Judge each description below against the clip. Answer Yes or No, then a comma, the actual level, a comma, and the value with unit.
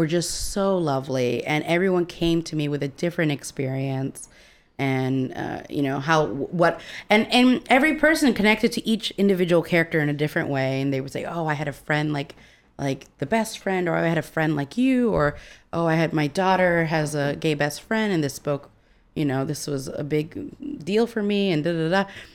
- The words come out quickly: Yes, fast, 215 wpm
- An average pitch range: Yes, average, 4.9 semitones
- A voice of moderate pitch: Yes, medium, 160 Hz